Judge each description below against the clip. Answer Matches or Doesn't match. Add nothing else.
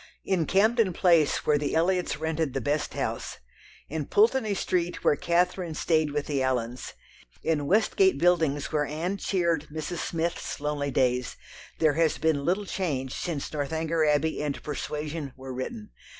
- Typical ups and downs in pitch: Matches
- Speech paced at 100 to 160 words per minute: Matches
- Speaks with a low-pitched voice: Doesn't match